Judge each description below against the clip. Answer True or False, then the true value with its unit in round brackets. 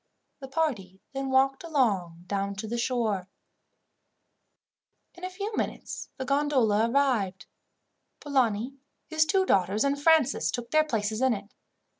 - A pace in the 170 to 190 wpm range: False (135 wpm)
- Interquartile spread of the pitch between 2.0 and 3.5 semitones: False (5.6 semitones)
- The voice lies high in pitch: True (255 Hz)